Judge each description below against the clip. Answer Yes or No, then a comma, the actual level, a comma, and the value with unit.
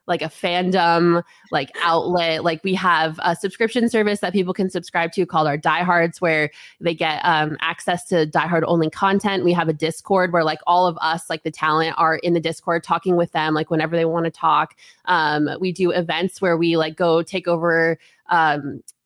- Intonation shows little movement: Yes, narrow, 1.9 semitones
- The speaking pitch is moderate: Yes, medium, 170 Hz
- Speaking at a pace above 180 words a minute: Yes, average, 200 wpm